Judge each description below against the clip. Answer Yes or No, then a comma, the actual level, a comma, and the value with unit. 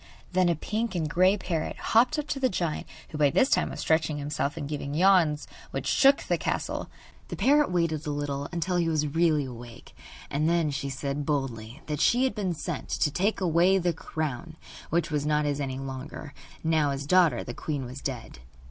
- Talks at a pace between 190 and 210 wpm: Yes, average, 200 wpm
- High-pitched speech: No, medium, 155 Hz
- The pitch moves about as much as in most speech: Yes, average, 3.7 semitones